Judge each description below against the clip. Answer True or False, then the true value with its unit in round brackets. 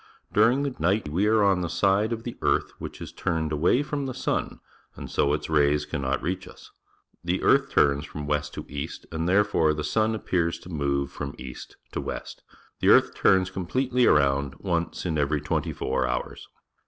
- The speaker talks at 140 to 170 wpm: False (190 wpm)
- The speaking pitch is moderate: False (85 Hz)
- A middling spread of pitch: False (5.9 semitones)